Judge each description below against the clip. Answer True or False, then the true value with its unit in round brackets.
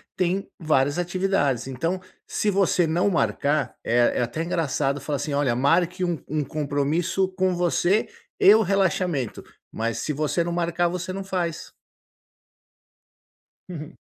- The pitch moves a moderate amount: True (4.2 semitones)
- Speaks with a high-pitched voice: False (170 Hz)